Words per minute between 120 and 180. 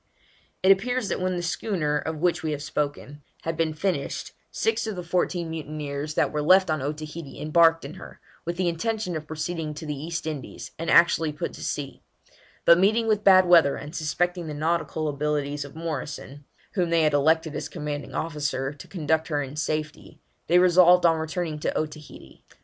No: average, 190 wpm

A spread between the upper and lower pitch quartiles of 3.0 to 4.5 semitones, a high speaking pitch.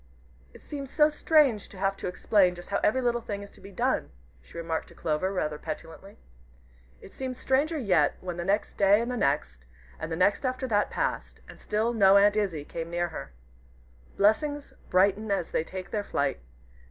No: average, 5.3 semitones; high, 200 Hz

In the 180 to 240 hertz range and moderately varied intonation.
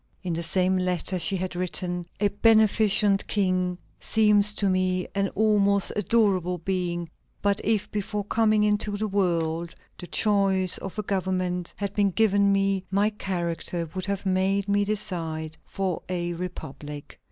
No: high, 190 Hz; narrow, 2.3 semitones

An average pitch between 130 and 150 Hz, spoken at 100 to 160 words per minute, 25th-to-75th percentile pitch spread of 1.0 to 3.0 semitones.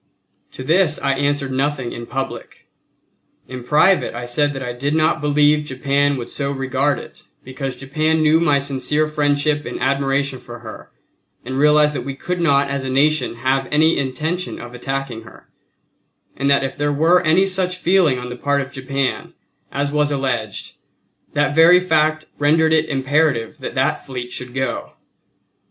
No: medium, 140 Hz; average, 170 wpm; narrow, 2.5 semitones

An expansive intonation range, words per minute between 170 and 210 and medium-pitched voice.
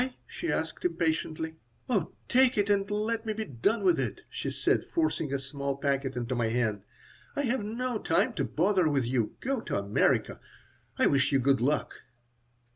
Yes: wide, 8.3 semitones; average, 180 wpm; medium, 160 Hz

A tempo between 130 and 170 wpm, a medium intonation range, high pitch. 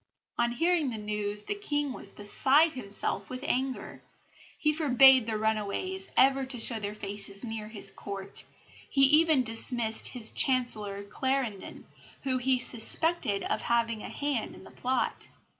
Yes: average, 150 wpm; average, 4.3 semitones; high, 245 Hz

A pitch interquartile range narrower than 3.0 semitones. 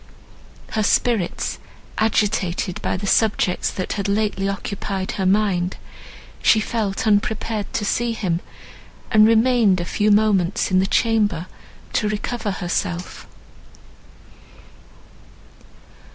Yes: narrow, 2.6 semitones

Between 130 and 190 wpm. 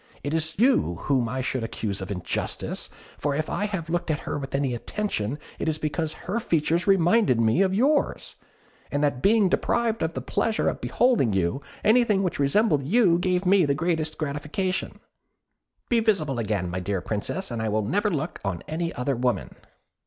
Yes: average, 185 wpm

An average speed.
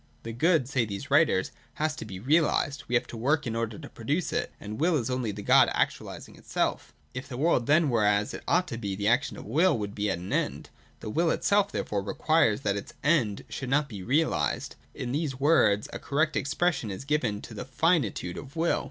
No: fast, 220 wpm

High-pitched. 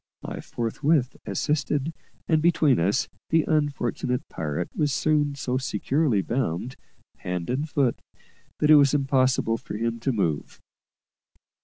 No: low, 130 Hz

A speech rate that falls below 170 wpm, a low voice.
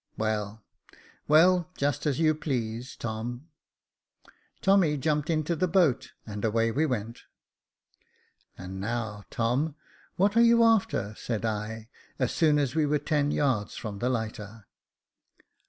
Yes: average, 140 wpm; low, 125 Hz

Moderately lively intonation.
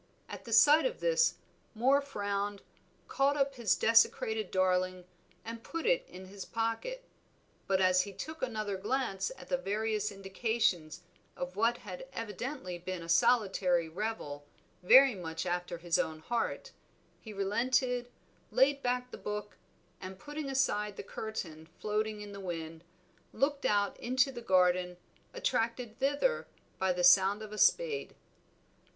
No: wide, 5.7 semitones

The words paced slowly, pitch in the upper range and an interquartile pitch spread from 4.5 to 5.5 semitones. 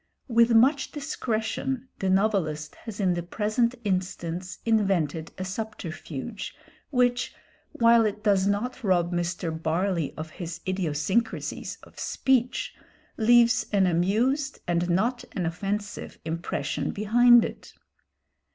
Yes: slow, 115 wpm; high, 200 Hz; average, 5.2 semitones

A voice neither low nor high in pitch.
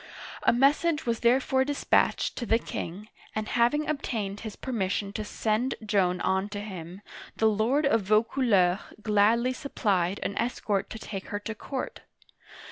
No: high, 215 Hz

